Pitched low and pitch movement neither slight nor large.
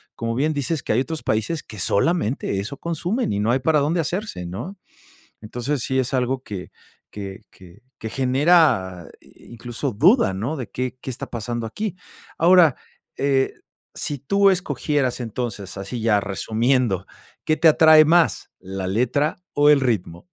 No: low, 130 Hz; wide, 6.2 semitones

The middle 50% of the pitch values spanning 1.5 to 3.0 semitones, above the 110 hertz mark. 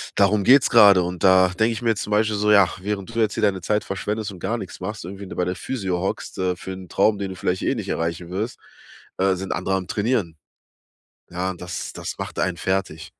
No: narrow, 2.6 semitones; very low, 95 Hz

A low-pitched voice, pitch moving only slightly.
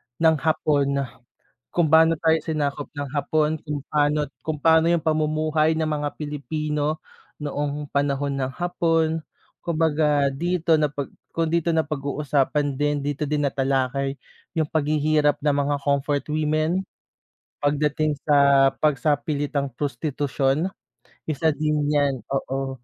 No: medium, 150 Hz; narrow, 1.7 semitones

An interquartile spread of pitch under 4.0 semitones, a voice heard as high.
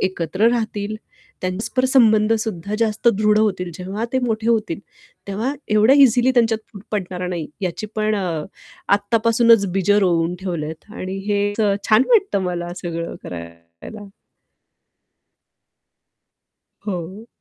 Yes: average, 3.6 semitones; high, 205 Hz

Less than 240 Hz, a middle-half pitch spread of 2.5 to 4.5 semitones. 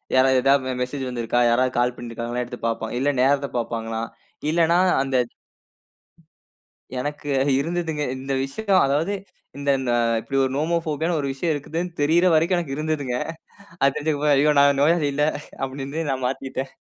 Yes: medium, 140 Hz; average, 3.3 semitones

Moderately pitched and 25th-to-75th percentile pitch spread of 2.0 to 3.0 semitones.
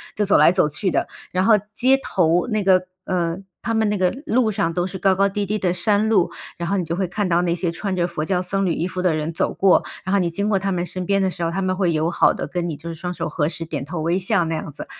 Yes: medium, 180 Hz; average, 2.7 semitones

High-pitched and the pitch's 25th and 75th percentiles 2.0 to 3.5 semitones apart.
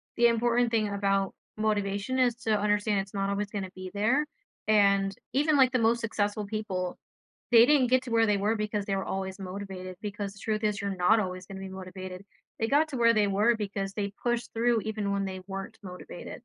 Yes: high, 205 Hz; average, 2.7 semitones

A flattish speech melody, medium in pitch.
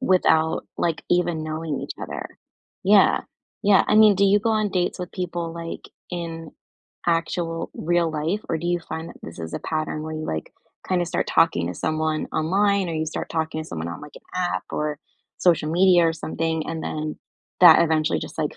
Yes: narrow, 2.1 semitones; medium, 165 Hz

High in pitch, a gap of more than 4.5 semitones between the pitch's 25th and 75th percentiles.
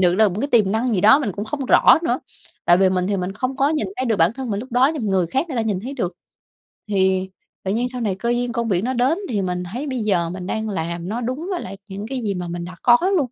Yes: high, 215 Hz; average, 5.1 semitones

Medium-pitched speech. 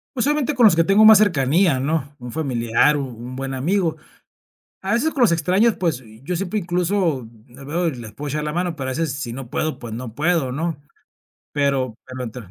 Yes: medium, 150 Hz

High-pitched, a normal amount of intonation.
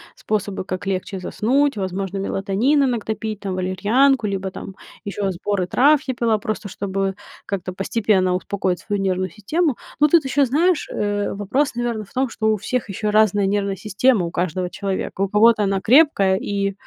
Yes: high, 205 Hz; average, 3.5 semitones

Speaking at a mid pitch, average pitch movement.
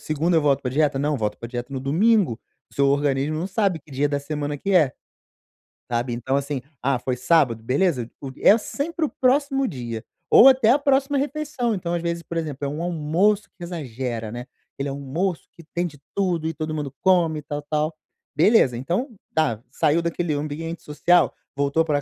Yes: medium, 155 Hz; average, 4.6 semitones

